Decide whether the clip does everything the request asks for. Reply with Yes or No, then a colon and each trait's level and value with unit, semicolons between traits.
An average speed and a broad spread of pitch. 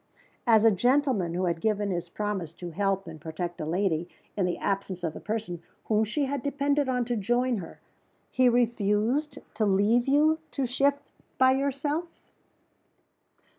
Yes: average, 165 wpm; wide, 6.0 semitones